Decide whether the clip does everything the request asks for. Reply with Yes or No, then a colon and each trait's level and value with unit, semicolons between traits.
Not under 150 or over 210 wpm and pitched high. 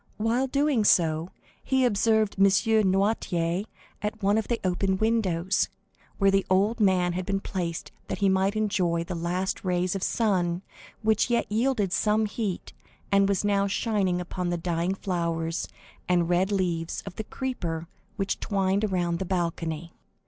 Yes: average, 160 wpm; high, 195 Hz